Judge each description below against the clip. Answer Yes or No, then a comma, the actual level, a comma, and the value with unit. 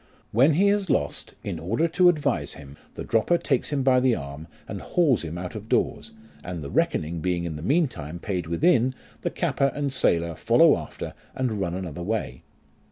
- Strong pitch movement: Yes, wide, 8.5 semitones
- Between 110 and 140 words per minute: No, average, 190 wpm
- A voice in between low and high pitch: No, low, 105 Hz